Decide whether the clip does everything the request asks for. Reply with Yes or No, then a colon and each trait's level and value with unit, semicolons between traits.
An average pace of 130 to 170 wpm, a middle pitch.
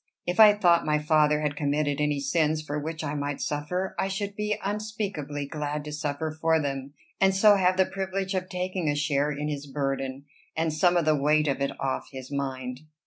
No: fast, 205 wpm; medium, 150 Hz